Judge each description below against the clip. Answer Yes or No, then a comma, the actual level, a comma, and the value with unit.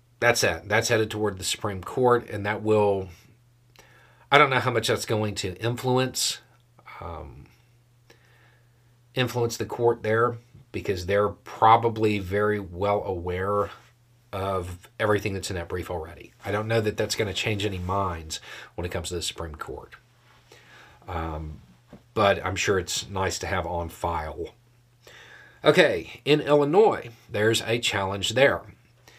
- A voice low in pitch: Yes, low, 110 Hz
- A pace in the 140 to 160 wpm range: Yes, average, 145 wpm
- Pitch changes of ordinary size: Yes, average, 3.6 semitones